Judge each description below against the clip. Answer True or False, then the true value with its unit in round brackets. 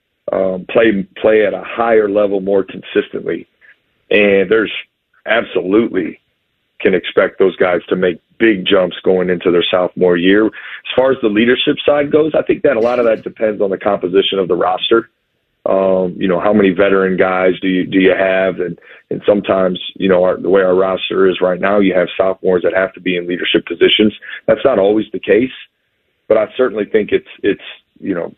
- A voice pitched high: False (95 Hz)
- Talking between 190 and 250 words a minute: True (200 wpm)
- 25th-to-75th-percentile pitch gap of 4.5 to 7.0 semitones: False (2.7 semitones)